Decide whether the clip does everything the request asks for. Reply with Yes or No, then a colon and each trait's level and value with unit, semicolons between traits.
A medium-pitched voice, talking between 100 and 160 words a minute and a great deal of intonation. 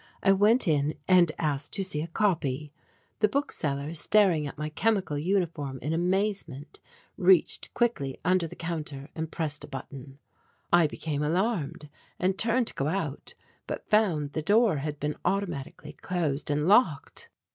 No: medium, 160 Hz; average, 155 wpm; average, 4.7 semitones